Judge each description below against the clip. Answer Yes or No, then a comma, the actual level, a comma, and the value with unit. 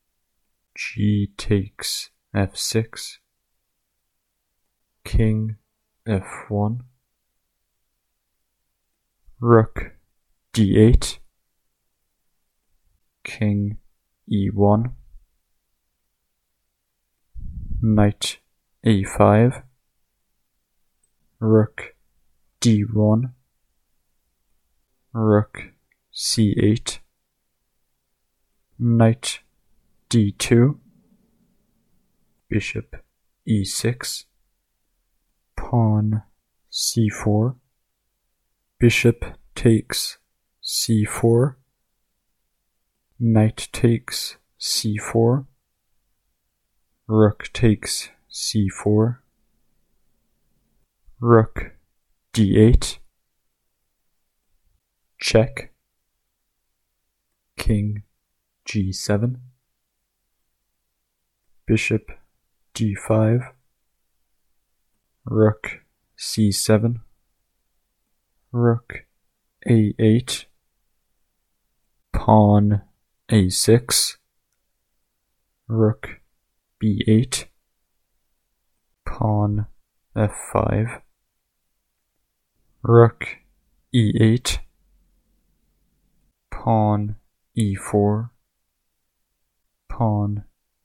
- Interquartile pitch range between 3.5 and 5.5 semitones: No, average, 2.7 semitones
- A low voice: Yes, low, 110 Hz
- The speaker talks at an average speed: No, slow, 45 wpm